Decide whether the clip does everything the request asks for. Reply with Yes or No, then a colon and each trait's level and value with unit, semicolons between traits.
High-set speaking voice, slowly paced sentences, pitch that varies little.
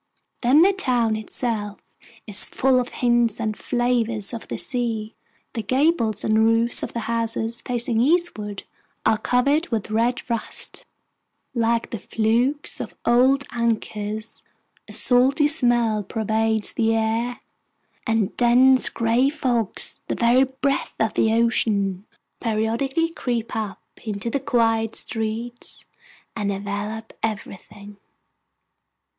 Yes: high, 230 Hz; slow, 120 wpm; narrow, 2.1 semitones